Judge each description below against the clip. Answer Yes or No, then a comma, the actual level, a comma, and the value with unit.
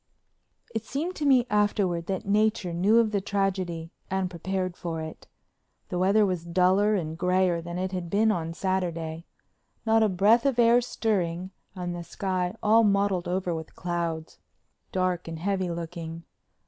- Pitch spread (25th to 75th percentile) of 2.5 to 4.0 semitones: Yes, average, 3.2 semitones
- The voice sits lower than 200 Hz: Yes, medium, 185 Hz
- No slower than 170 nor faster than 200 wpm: No, average, 160 wpm